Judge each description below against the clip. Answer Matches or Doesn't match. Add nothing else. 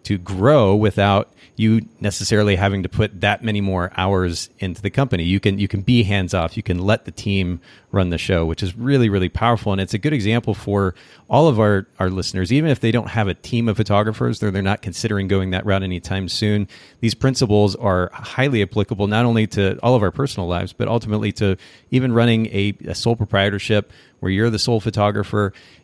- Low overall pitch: Matches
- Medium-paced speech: Doesn't match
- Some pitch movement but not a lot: Matches